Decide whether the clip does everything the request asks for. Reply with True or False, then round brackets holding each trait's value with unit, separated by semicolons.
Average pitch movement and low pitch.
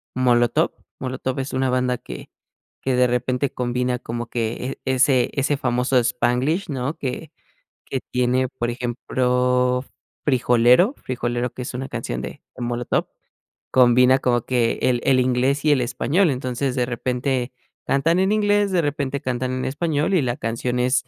False (1.7 semitones; 125 Hz)